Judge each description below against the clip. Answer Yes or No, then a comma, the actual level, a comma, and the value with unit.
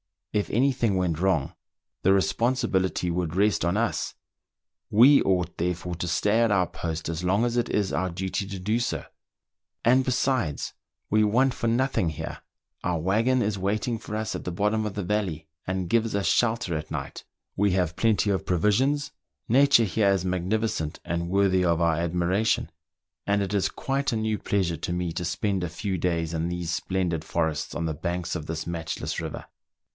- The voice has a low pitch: Yes, very low, 95 Hz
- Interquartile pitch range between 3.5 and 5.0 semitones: Yes, average, 4.1 semitones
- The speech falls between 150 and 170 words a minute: No, average, 185 wpm